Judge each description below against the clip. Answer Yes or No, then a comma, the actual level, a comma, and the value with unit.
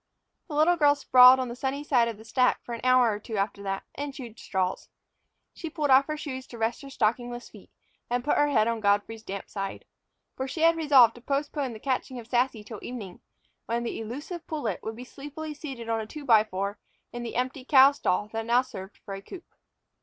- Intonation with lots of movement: No, average, 4.1 semitones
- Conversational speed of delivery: No, fast, 225 wpm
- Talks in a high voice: Yes, high, 245 Hz